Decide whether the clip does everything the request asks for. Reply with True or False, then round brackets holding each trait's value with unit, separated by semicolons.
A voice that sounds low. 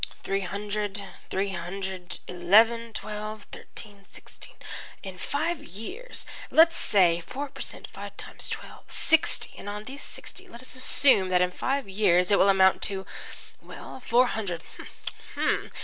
False (205 Hz)